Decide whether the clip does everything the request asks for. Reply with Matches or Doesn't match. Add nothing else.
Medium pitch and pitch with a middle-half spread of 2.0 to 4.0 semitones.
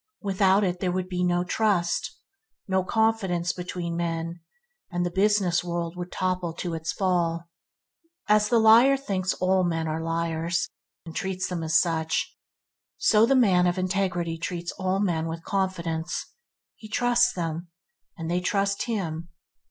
Matches